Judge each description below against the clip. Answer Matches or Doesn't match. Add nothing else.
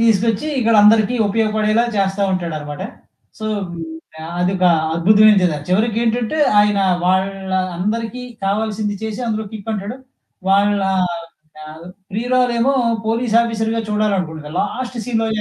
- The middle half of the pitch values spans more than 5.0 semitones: Doesn't match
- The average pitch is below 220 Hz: Matches